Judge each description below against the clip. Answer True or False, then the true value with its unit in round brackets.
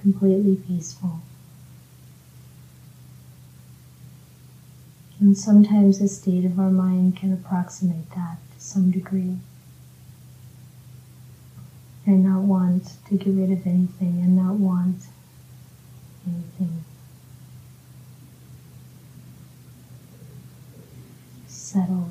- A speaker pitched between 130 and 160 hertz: True (135 Hz)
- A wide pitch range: True (6.2 semitones)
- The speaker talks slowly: True (75 wpm)